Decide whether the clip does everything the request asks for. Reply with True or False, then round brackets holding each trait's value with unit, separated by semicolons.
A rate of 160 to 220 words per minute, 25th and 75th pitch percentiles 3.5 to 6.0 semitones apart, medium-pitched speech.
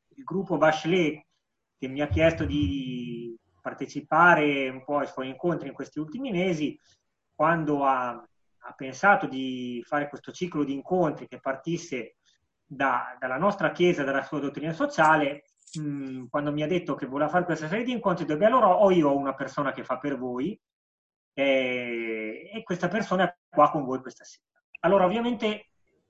True (170 wpm; 4.8 semitones; 150 Hz)